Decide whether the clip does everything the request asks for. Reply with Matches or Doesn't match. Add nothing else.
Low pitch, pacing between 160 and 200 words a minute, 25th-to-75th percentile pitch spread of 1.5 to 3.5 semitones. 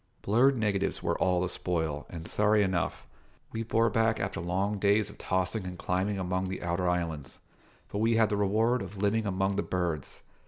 Matches